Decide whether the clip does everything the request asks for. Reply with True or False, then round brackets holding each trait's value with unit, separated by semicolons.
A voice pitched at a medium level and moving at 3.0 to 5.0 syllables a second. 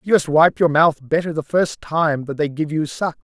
True (155 Hz; 4.8 syllables/s)